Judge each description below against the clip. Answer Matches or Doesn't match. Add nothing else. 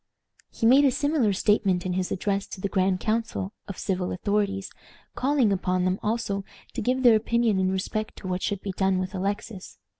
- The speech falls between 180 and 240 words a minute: Matches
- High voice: Matches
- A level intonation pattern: Doesn't match